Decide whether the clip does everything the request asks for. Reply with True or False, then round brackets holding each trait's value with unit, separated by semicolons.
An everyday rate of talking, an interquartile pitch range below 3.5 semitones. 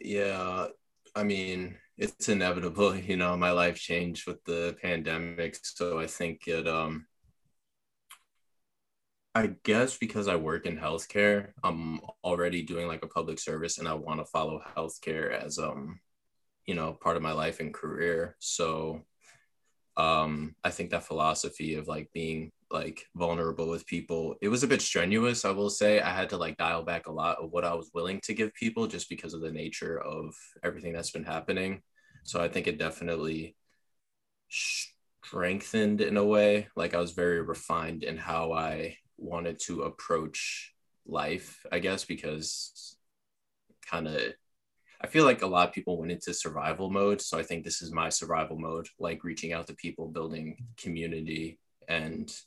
True (170 wpm; 2.4 semitones)